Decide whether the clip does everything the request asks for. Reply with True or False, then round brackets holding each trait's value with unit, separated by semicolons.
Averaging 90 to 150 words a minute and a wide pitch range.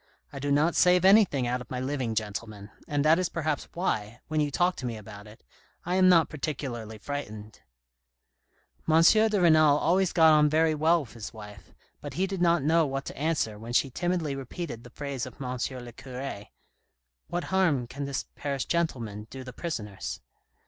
False (190 wpm; 5.8 semitones)